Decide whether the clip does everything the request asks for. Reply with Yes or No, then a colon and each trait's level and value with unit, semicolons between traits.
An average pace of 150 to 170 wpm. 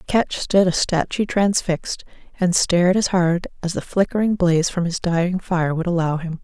No: average, 185 wpm